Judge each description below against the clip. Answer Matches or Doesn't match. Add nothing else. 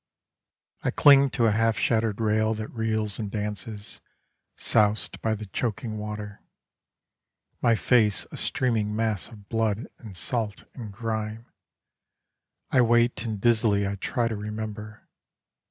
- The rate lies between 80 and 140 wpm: Matches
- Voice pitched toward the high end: Doesn't match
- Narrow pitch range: Matches